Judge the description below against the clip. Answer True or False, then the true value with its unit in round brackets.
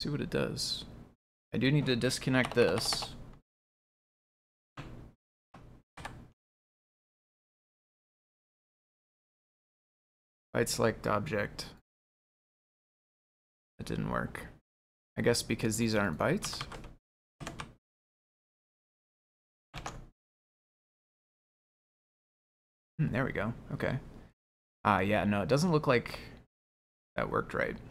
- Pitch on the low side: True (105 Hz)